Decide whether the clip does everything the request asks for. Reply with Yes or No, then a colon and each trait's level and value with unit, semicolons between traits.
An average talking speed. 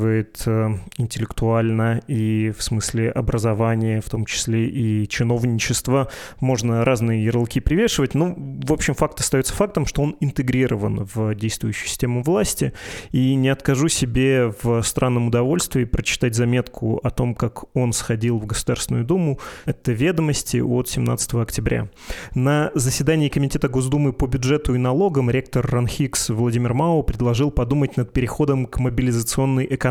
Yes: average, 135 wpm